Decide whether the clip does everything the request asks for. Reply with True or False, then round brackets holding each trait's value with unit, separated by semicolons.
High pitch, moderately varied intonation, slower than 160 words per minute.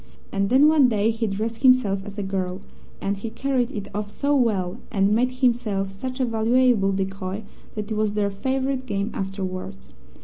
False (210 Hz; 4.2 semitones; 180 wpm)